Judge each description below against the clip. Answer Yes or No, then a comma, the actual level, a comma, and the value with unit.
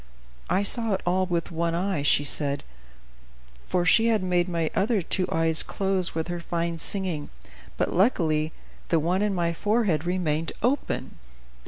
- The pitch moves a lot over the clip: No, average, 2.9 semitones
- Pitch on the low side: No, medium, 175 Hz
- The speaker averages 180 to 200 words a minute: No, average, 160 wpm